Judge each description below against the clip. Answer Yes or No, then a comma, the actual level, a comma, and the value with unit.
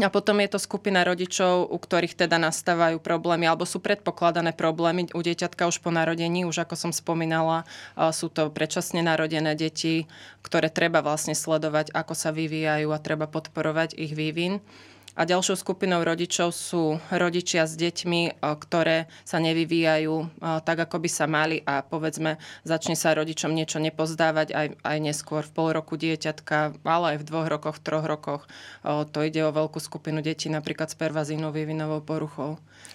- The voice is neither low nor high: Yes, medium, 160 Hz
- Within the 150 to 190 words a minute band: Yes, fast, 165 wpm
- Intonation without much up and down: Yes, narrow, 1.5 semitones